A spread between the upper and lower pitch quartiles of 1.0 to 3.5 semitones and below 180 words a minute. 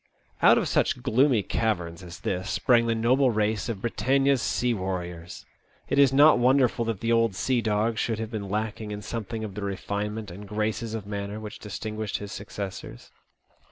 No: narrow, 2.5 semitones; average, 185 wpm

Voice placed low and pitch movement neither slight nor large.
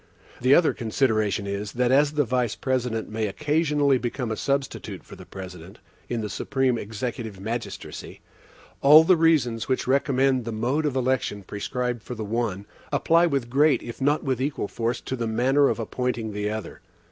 Yes: low, 125 Hz; average, 3.8 semitones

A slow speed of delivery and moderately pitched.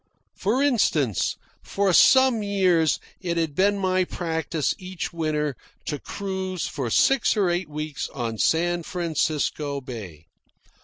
Yes: slow, 125 wpm; medium, 170 Hz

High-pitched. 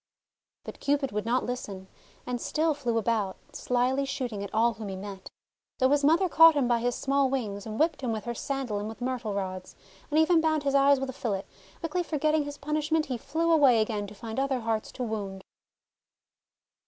Yes: very high, 255 Hz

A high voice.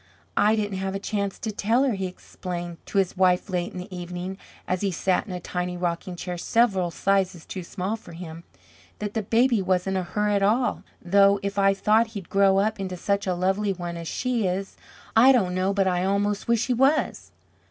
Yes: high, 195 Hz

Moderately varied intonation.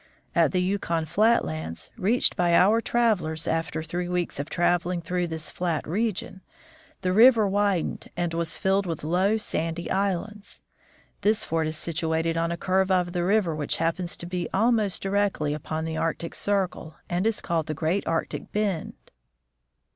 Yes: average, 3.5 semitones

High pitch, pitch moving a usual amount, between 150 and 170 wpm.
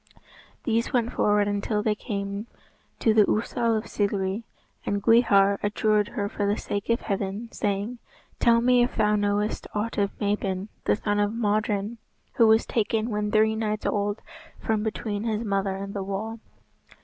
No: high, 210 Hz; narrow, 1.7 semitones; average, 165 wpm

